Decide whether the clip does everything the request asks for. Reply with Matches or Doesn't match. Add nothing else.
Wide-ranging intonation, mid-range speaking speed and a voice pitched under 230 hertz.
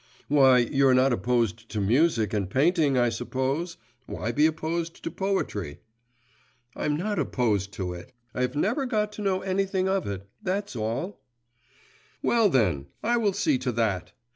Matches